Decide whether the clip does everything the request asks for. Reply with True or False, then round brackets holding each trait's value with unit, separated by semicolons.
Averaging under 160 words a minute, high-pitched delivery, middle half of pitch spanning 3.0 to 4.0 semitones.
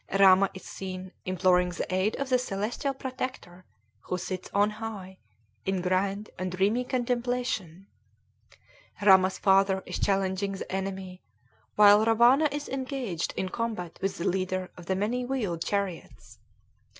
True (140 wpm; 195 Hz; 3.7 semitones)